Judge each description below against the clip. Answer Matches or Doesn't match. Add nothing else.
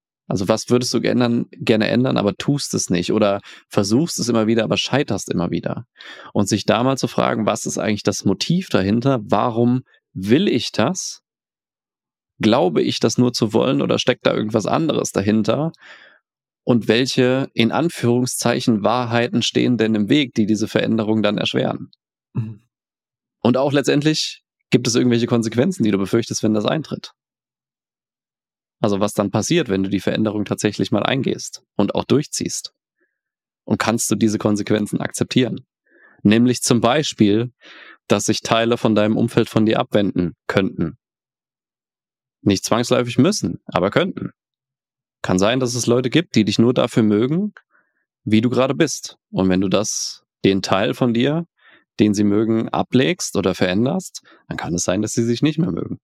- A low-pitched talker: Matches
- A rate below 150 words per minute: Doesn't match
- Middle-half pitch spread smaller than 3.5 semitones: Matches